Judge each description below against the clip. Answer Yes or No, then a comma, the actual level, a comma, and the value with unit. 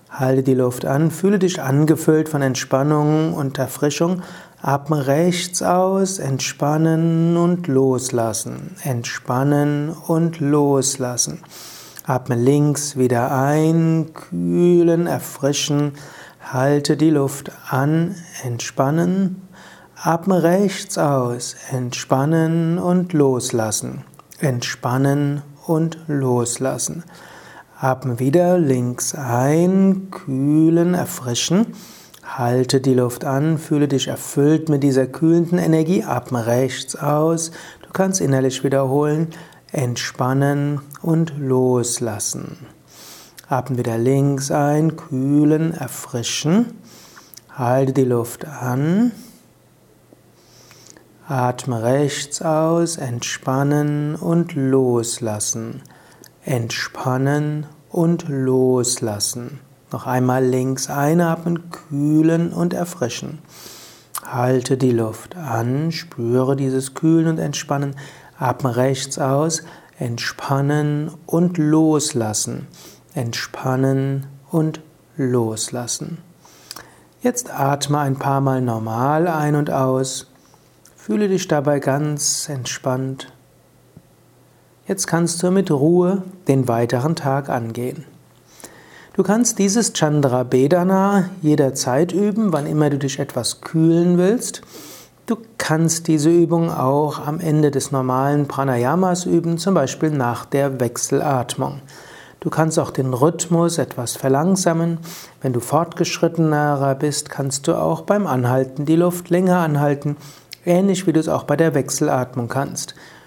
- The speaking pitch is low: No, medium, 145 Hz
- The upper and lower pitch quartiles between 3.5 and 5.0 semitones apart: Yes, average, 4.1 semitones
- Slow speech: Yes, slow, 100 wpm